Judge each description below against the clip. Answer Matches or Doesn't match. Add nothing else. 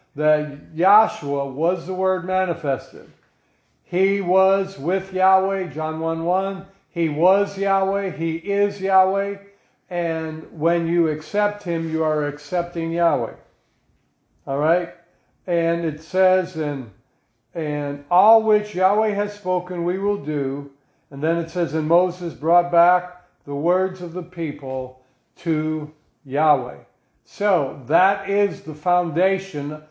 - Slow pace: Matches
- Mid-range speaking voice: Matches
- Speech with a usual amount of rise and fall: Matches